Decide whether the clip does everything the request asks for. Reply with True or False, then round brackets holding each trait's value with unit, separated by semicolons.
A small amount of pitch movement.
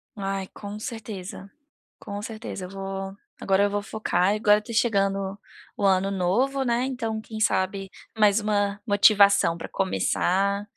True (1.9 semitones)